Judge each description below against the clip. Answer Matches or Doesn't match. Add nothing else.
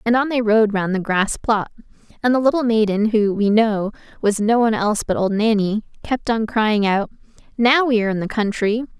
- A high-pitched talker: Matches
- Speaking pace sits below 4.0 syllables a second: Doesn't match